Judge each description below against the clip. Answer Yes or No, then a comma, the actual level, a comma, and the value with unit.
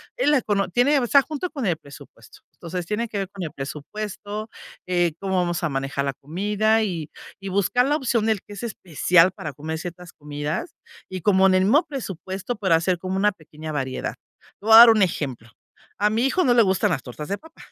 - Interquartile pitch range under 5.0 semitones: No, average, 5.3 semitones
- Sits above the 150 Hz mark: Yes, high, 190 Hz